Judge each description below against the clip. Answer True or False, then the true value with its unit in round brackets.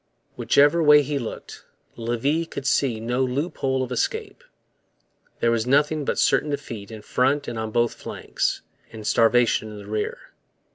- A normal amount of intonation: True (4.0 semitones)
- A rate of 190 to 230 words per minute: False (155 wpm)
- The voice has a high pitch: False (125 Hz)